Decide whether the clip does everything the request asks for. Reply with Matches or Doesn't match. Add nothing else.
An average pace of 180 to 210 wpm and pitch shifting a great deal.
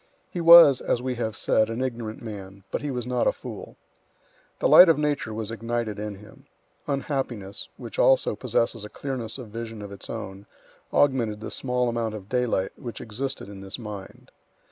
Doesn't match